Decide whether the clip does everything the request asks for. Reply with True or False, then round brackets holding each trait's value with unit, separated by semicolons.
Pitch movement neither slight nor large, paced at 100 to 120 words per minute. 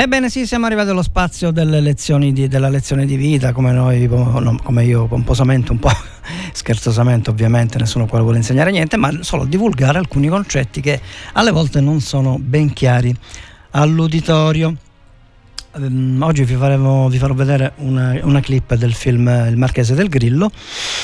False (3.6 semitones; 155 wpm)